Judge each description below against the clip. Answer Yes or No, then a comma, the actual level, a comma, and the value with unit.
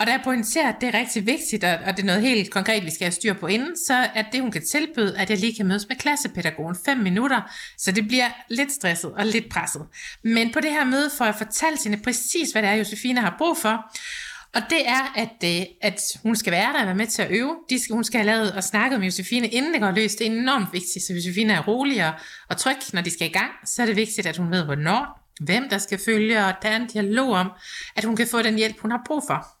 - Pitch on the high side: Yes, high, 220 Hz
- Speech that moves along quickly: Yes, fast, 270 wpm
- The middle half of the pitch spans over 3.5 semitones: Yes, average, 4.2 semitones